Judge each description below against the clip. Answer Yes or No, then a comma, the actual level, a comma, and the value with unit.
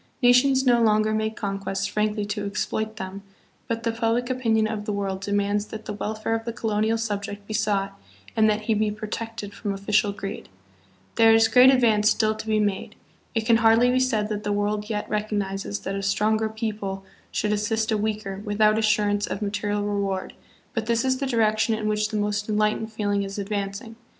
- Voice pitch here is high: Yes, high, 215 Hz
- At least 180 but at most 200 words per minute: Yes, average, 195 wpm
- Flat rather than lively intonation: Yes, narrow, 1.5 semitones